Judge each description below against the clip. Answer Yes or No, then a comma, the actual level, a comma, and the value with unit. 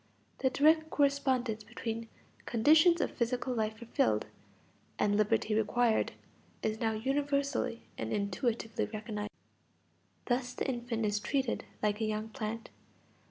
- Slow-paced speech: Yes, slow, 120 wpm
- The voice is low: No, high, 230 Hz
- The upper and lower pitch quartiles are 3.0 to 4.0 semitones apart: Yes, average, 3.5 semitones